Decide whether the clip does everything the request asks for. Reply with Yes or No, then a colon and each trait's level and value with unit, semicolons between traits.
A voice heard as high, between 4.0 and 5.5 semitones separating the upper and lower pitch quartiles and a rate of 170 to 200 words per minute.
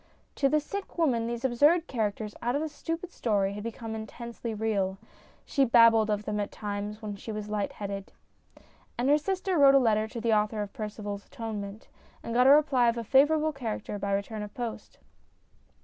Yes: high, 225 Hz; average, 4.5 semitones; average, 195 wpm